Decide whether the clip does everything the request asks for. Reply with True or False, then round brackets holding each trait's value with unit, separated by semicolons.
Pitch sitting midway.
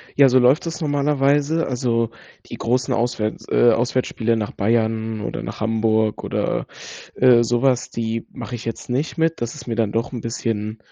False (120 Hz)